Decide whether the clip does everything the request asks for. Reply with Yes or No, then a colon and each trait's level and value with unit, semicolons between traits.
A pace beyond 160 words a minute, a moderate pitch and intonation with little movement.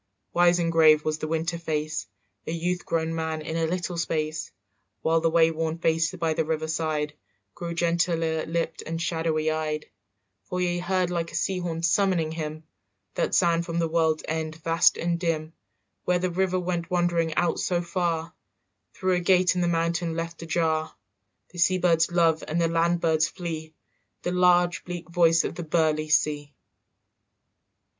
Yes: average, 170 wpm; medium, 165 Hz; narrow, 1.5 semitones